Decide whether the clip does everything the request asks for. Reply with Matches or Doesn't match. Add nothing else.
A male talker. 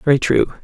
Matches